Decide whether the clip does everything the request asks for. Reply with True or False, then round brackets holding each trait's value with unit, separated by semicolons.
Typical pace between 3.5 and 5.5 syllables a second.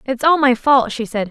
True (5.0 syllables/s)